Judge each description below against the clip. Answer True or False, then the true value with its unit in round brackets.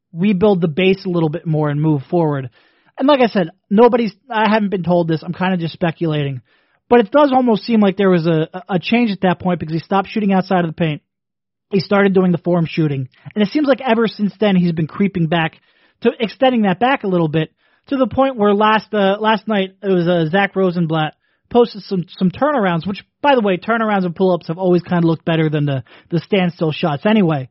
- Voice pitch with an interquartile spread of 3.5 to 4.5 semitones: True (4.2 semitones)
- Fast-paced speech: True (240 wpm)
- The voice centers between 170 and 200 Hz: True (185 Hz)